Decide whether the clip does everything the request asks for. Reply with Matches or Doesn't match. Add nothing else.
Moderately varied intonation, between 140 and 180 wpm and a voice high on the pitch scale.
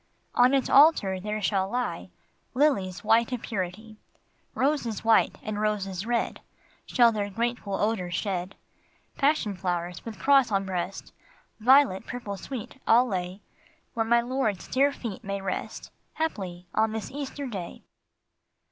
Matches